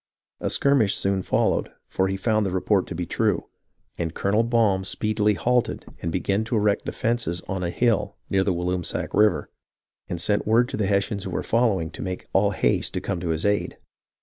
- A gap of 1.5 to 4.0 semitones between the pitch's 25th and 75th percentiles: Yes, average, 2.9 semitones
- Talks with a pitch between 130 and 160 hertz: No, low, 100 Hz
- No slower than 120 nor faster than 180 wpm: No, average, 200 wpm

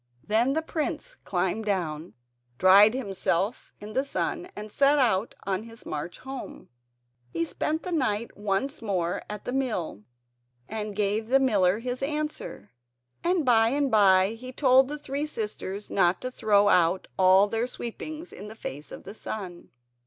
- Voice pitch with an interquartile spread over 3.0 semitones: Yes, wide, 5.6 semitones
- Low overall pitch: No, high, 220 Hz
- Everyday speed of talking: Yes, average, 160 wpm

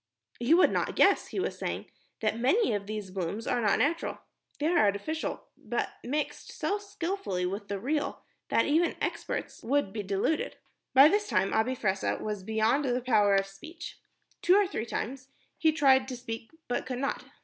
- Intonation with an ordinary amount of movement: No, wide, 6.9 semitones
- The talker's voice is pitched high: Yes, high, 245 Hz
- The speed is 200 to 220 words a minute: No, average, 180 wpm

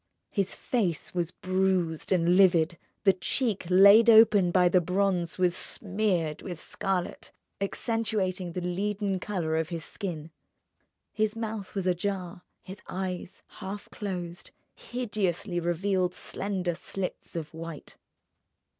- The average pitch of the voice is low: No, medium, 185 Hz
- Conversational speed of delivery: No, slow, 120 wpm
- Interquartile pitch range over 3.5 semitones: No, narrow, 2.5 semitones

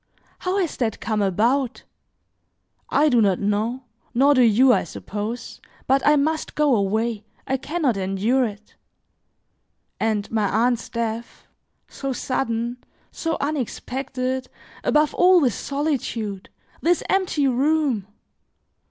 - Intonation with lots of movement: No, average, 4.4 semitones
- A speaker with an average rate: No, slow, 125 wpm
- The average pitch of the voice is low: No, very high, 250 Hz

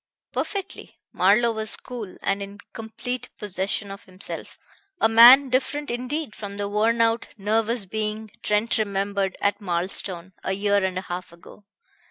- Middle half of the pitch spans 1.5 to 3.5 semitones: Yes, average, 2.8 semitones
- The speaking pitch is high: Yes, high, 210 Hz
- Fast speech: No, average, 150 wpm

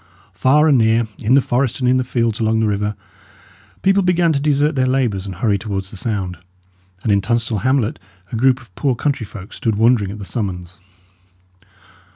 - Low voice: Yes, low, 115 Hz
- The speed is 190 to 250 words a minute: Yes, average, 195 wpm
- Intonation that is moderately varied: Yes, average, 4.3 semitones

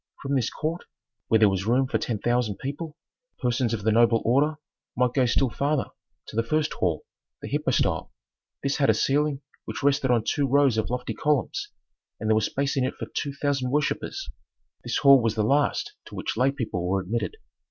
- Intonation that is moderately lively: Yes, average, 3.9 semitones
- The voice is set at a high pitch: No, low, 130 Hz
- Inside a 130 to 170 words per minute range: No, average, 200 wpm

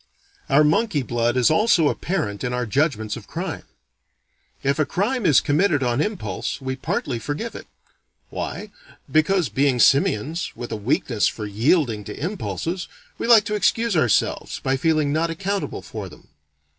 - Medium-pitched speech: Yes, medium, 145 Hz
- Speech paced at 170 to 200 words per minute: No, average, 155 wpm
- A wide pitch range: Yes, wide, 6.6 semitones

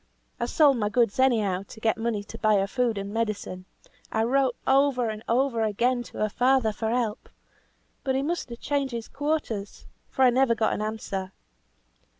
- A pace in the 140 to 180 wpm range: No, average, 190 wpm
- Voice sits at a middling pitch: No, high, 230 Hz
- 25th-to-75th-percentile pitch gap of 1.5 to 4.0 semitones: Yes, average, 3.6 semitones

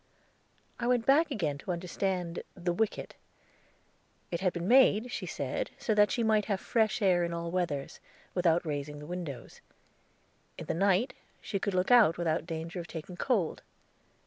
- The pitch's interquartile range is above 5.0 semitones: No, average, 4.1 semitones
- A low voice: No, medium, 180 Hz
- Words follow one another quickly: No, average, 170 wpm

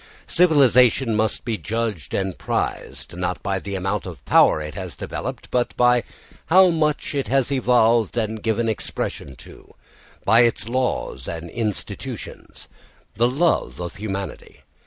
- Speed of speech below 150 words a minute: Yes, average, 140 wpm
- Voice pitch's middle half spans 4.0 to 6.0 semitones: Yes, average, 4.5 semitones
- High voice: No, low, 115 Hz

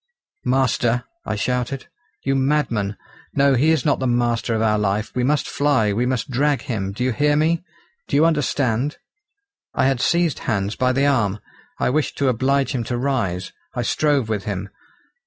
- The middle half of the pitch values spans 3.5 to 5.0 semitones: Yes, average, 4.0 semitones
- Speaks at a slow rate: No, average, 180 wpm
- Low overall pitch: Yes, low, 125 Hz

